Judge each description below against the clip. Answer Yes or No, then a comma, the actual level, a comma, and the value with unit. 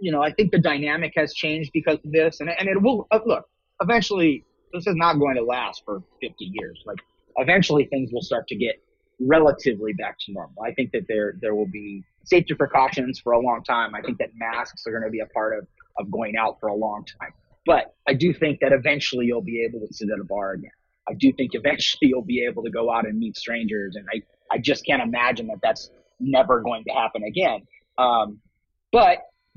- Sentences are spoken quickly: Yes, fast, 225 wpm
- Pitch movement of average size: No, wide, 6.0 semitones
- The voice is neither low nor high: Yes, medium, 145 Hz